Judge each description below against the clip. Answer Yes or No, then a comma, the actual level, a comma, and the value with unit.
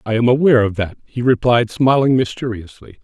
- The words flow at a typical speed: Yes, average, 160 wpm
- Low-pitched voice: Yes, low, 115 Hz